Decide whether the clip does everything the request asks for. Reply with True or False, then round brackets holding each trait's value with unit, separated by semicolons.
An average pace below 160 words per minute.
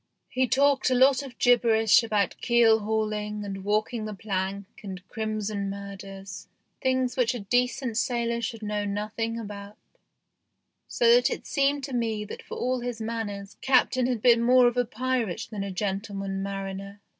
False (165 wpm)